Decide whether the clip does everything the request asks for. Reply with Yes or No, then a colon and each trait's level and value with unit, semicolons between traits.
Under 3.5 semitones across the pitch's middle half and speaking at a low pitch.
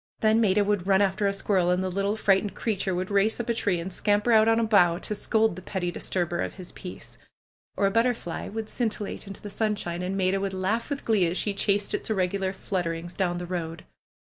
No: average, 2.7 semitones; high, 195 Hz